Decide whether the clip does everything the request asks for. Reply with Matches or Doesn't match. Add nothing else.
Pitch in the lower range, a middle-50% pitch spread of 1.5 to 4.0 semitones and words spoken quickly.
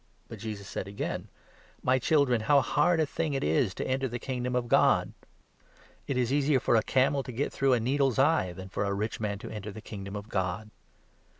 Doesn't match